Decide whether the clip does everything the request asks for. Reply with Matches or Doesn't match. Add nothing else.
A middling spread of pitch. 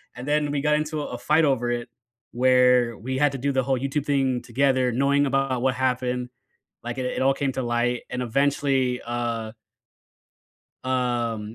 Doesn't match